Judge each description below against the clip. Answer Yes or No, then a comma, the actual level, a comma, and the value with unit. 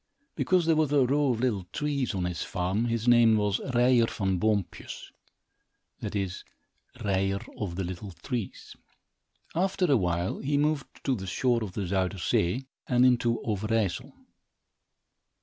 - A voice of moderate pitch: No, low, 110 Hz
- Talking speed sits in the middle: Yes, average, 150 wpm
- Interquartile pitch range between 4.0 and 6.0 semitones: Yes, average, 5.2 semitones